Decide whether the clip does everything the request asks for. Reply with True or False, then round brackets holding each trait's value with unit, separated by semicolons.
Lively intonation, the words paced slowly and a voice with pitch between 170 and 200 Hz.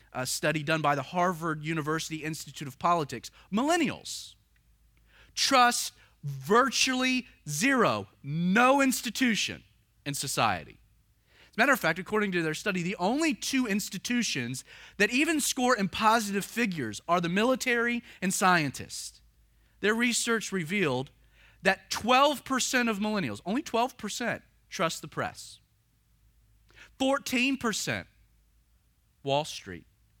True (8.8 semitones; 115 wpm; 190 Hz)